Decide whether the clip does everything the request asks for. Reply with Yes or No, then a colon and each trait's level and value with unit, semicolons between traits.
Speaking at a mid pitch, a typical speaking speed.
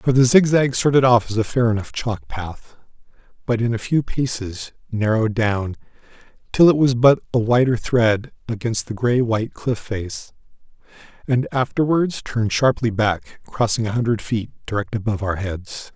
No: low, 115 Hz; average, 165 wpm